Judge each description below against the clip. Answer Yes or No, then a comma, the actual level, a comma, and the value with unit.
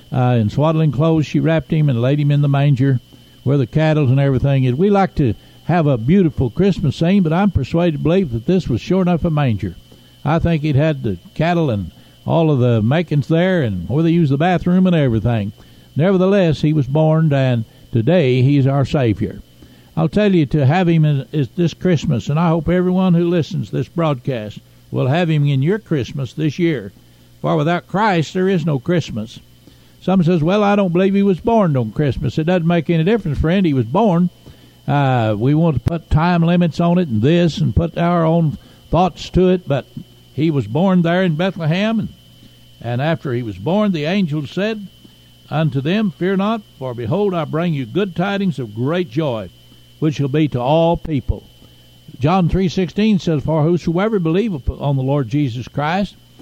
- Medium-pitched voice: Yes, medium, 155 Hz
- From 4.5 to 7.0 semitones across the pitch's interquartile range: Yes, average, 5.0 semitones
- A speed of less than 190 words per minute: No, average, 200 wpm